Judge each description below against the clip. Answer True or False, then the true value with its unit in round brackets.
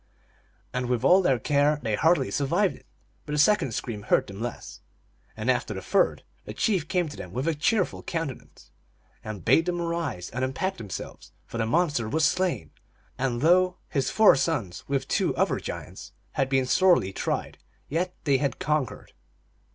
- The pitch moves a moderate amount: False (6.0 semitones)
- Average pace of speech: True (175 wpm)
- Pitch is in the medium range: True (145 Hz)